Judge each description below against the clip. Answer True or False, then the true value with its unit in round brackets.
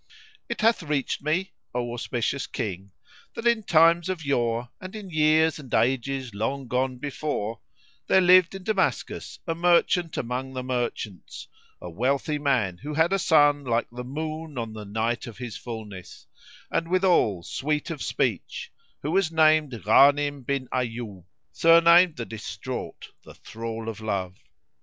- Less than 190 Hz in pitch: True (135 Hz)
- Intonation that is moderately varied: False (5.7 semitones)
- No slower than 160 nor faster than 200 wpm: False (150 wpm)